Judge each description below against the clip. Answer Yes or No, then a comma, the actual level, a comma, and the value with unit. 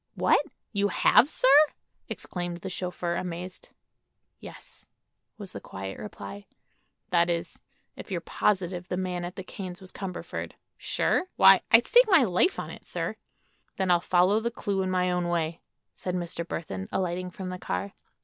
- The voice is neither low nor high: Yes, medium, 180 Hz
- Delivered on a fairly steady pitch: Yes, narrow, 1.8 semitones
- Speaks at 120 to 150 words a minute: No, average, 165 wpm